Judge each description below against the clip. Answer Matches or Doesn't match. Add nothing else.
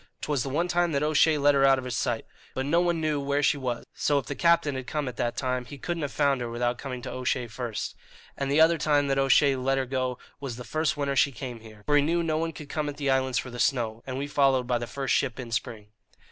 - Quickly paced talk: Matches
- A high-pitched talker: Doesn't match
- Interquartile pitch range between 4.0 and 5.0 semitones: Doesn't match